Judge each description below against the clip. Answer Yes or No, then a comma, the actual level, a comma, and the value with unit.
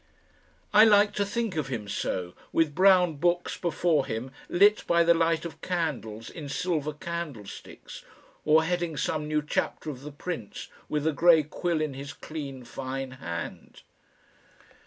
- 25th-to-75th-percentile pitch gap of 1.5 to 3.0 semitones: No, average, 4.1 semitones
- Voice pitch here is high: No, medium, 155 Hz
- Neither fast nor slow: Yes, average, 155 wpm